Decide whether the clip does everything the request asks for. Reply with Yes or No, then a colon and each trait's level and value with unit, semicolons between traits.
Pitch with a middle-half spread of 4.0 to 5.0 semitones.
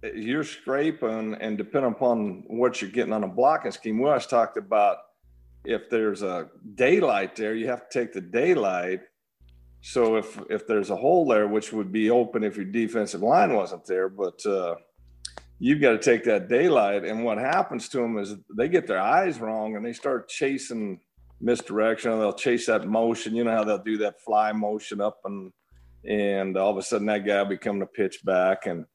No: average, 2.8 semitones